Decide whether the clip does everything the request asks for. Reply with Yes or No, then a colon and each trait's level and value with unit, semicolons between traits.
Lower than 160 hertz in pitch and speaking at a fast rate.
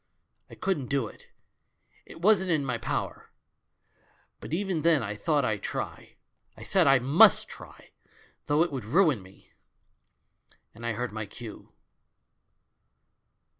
No: low, 135 Hz; slow, 135 wpm